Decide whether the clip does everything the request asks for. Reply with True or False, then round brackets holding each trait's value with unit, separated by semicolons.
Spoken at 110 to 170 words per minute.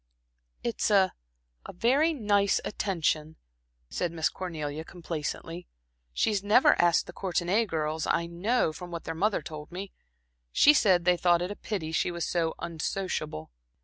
True (150 wpm)